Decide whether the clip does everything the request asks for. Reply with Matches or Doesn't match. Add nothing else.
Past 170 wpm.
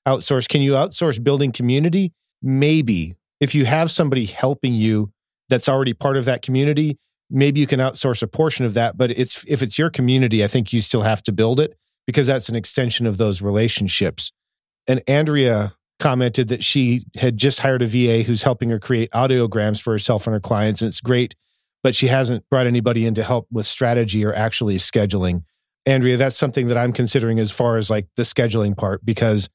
Matches